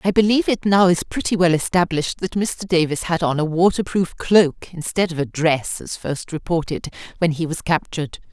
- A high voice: No, medium, 170 Hz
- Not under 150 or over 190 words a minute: No, average, 200 wpm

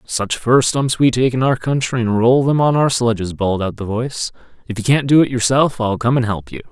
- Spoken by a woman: No, male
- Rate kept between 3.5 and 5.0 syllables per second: No, 5.5 syllables/s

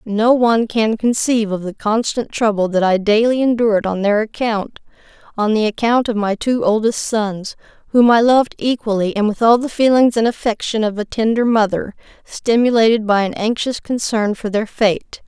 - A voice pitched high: Yes, high, 220 Hz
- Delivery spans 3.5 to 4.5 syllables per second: No, 5.0 syllables/s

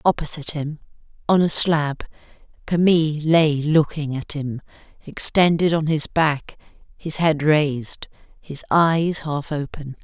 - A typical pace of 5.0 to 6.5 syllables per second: No, 4.1 syllables/s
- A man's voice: No, female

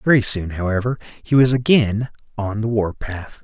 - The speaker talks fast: No, average, 175 wpm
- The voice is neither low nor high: No, low, 110 Hz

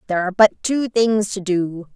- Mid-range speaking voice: No, high, 200 Hz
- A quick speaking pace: Yes, fast, 215 wpm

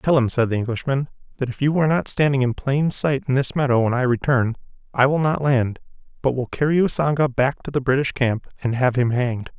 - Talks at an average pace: No, fast, 230 wpm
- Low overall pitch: Yes, low, 130 Hz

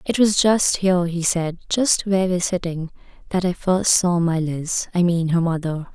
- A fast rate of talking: No, average, 190 wpm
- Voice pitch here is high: No, medium, 175 Hz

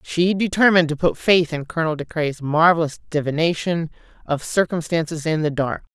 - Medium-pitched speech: Yes, medium, 160 Hz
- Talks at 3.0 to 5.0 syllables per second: No, 5.5 syllables/s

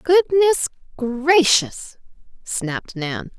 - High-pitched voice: Yes, very high, 265 Hz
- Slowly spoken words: Yes, slow, 70 wpm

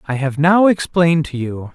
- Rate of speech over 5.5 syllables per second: No, 5.0 syllables/s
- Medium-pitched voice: Yes, medium, 155 Hz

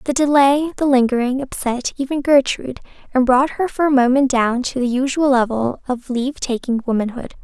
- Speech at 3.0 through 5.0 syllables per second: No, 5.3 syllables/s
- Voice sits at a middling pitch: No, very high, 260 Hz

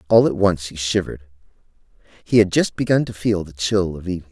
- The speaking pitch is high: No, very low, 95 Hz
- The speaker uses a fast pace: Yes, fast, 210 wpm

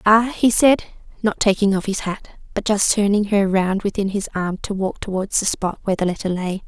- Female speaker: Yes, female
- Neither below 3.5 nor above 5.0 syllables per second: No, 5.3 syllables/s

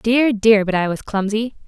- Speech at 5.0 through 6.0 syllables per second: No, 4.6 syllables/s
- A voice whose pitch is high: Yes, high, 215 Hz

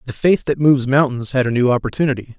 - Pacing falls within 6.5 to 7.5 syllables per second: Yes, 6.9 syllables/s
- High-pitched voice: No, low, 130 Hz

